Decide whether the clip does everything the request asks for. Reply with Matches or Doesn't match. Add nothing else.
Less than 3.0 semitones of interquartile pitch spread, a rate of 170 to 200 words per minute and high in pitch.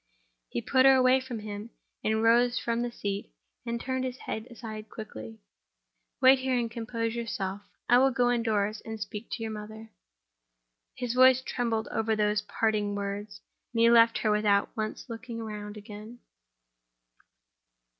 Doesn't match